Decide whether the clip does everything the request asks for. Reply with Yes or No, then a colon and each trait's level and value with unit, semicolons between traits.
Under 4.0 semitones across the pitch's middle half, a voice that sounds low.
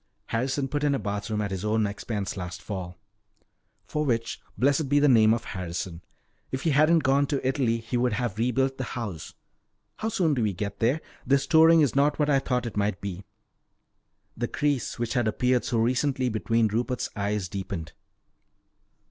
No: average, 4.8 semitones; low, 120 Hz